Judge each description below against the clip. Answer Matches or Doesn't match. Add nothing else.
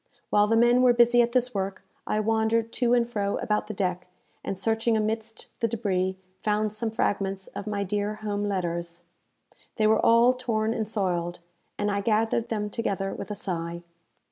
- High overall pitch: Matches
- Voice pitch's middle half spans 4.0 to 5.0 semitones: Doesn't match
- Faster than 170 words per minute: Matches